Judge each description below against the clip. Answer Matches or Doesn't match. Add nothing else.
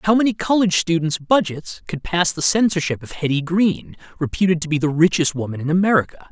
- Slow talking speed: Doesn't match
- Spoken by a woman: Doesn't match